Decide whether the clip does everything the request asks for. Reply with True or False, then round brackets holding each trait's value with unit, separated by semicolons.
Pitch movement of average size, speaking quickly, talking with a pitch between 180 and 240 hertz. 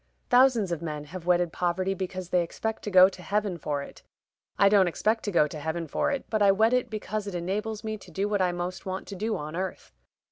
True (3.4 semitones; 245 wpm; 185 Hz)